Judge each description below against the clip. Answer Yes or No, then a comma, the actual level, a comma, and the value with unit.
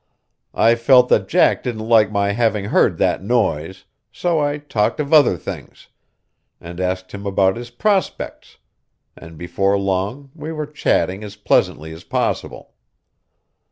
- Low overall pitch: Yes, low, 105 Hz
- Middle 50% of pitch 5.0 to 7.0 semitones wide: Yes, wide, 5.5 semitones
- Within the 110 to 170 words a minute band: Yes, average, 145 wpm